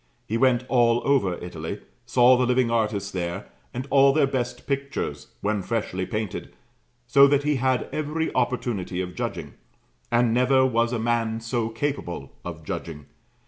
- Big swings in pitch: No, average, 3.7 semitones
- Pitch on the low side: Yes, low, 120 Hz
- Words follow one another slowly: No, average, 155 wpm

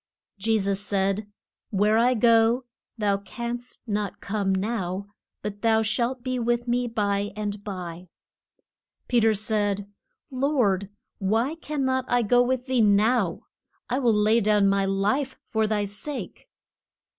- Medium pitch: No, high, 215 Hz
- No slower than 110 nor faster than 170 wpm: Yes, average, 145 wpm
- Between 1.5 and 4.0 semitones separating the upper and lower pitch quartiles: Yes, average, 3.2 semitones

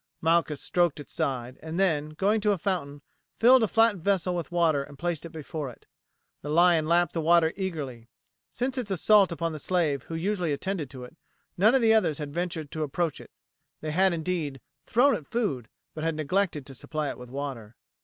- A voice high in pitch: No, medium, 165 Hz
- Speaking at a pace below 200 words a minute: No, fast, 205 wpm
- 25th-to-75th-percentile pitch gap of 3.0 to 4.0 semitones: No, average, 4.4 semitones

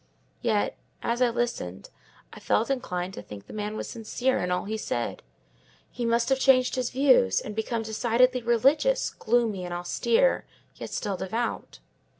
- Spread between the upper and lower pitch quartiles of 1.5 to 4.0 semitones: Yes, average, 3.5 semitones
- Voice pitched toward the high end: Yes, high, 230 Hz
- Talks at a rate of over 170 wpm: No, average, 160 wpm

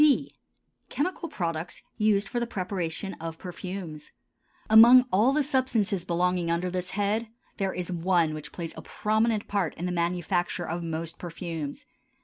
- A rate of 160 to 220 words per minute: No, average, 150 wpm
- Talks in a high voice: No, medium, 180 Hz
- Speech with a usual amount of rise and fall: Yes, average, 3.9 semitones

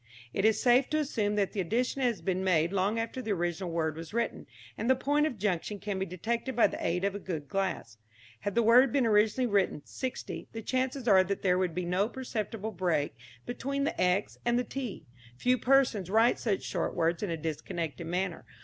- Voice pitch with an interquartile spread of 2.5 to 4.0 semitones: No, average, 5.1 semitones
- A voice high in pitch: Yes, high, 205 Hz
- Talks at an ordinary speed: No, fast, 210 wpm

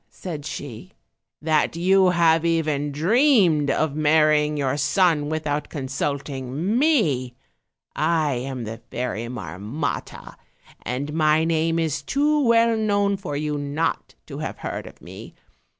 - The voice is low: No, medium, 155 Hz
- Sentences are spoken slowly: Yes, slow, 130 wpm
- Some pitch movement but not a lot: Yes, average, 3.3 semitones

